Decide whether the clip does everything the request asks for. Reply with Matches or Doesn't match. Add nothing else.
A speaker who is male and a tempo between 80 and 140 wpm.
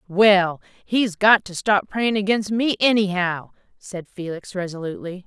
Doesn't match